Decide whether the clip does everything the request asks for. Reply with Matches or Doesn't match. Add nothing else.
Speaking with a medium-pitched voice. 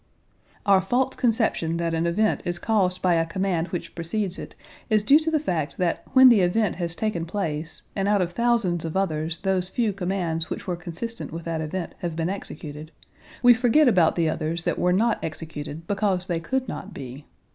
Matches